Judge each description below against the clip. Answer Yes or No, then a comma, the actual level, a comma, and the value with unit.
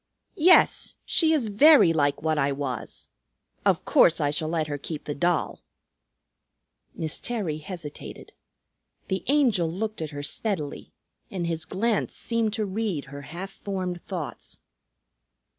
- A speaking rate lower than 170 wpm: Yes, average, 140 wpm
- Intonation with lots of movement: Yes, wide, 5.9 semitones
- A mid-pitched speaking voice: Yes, medium, 175 Hz